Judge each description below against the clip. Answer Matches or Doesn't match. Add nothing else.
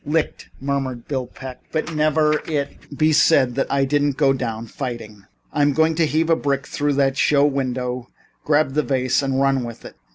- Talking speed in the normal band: Matches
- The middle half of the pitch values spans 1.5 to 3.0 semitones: Matches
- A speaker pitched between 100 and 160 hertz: Matches